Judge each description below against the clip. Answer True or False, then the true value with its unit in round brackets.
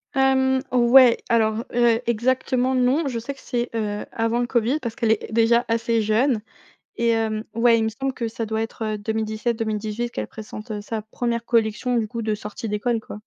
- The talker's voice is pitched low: False (230 Hz)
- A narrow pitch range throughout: True (1.9 semitones)